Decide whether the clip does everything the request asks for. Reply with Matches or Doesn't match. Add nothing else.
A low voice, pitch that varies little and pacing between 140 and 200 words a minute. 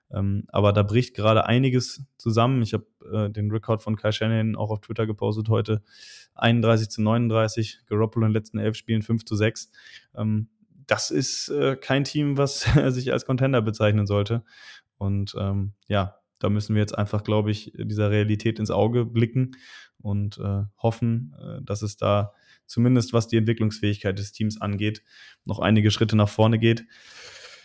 Matches